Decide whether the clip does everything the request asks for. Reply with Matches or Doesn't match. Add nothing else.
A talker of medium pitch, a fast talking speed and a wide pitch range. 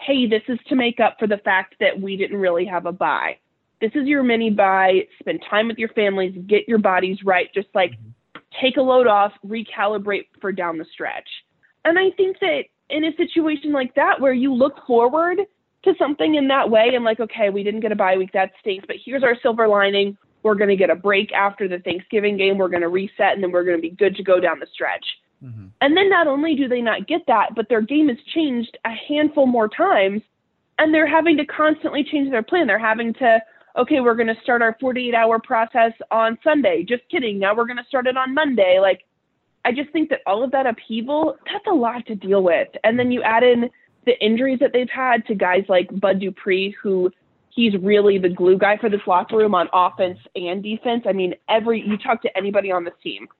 Doesn't match